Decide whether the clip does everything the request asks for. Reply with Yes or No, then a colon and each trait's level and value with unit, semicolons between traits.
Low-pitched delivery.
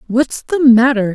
No: high, 245 Hz